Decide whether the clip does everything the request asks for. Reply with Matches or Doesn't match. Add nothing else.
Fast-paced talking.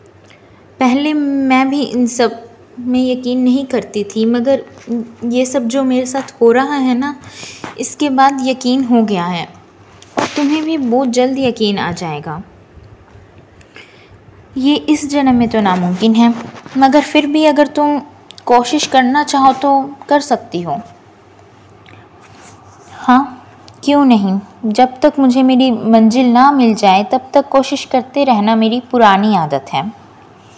Doesn't match